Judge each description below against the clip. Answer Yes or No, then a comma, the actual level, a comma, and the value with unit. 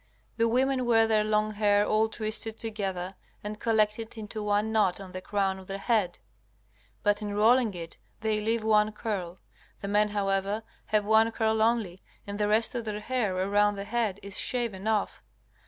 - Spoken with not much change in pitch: Yes, narrow, 1.6 semitones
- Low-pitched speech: No, high, 210 Hz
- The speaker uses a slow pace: No, average, 180 wpm